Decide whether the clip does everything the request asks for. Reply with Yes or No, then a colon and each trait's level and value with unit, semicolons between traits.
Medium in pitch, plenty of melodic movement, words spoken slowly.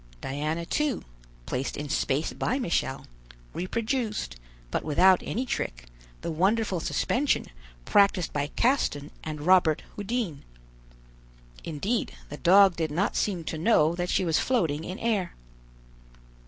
Yes: medium, 175 Hz; wide, 5.8 semitones; slow, 130 wpm